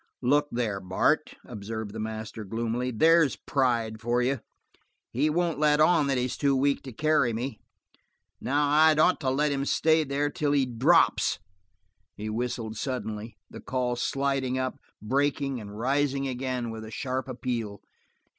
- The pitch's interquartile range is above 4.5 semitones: No, average, 4.0 semitones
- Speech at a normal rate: Yes, average, 155 wpm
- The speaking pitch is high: No, low, 130 Hz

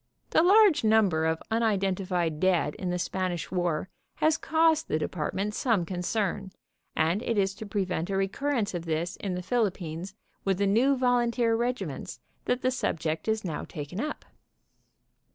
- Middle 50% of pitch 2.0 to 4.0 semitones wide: No, average, 5.0 semitones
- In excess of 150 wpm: Yes, average, 160 wpm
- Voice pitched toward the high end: Yes, high, 195 Hz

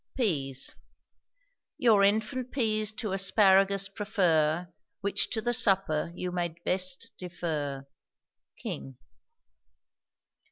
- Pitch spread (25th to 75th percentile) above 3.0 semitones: Yes, average, 4.2 semitones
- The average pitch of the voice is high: Yes, high, 195 Hz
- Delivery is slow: Yes, slow, 90 wpm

